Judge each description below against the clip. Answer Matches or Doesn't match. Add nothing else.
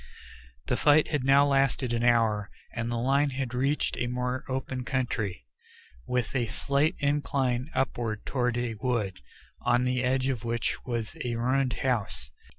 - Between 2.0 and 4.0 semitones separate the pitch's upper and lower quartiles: Matches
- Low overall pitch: Matches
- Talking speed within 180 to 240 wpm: Doesn't match